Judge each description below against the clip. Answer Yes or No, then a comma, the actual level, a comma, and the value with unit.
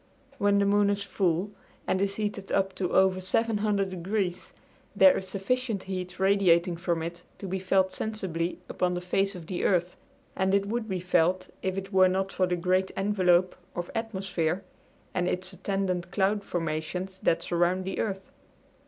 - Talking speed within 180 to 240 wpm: No, average, 170 wpm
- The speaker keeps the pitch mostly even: Yes, narrow, 1.8 semitones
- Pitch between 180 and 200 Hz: Yes, high, 190 Hz